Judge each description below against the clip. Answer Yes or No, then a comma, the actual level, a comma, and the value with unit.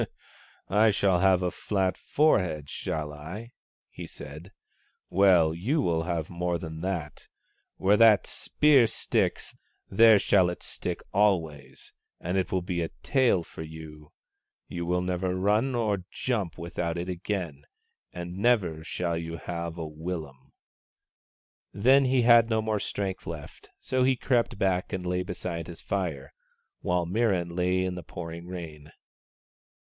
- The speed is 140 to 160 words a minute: Yes, average, 155 wpm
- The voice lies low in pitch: Yes, very low, 90 Hz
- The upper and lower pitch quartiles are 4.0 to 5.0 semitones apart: No, average, 3.5 semitones